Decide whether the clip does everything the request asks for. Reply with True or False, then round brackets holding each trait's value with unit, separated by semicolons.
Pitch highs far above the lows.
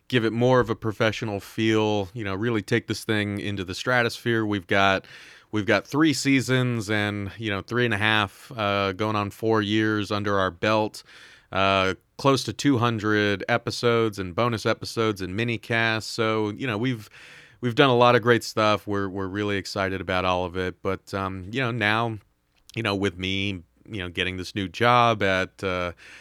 False (3.0 semitones)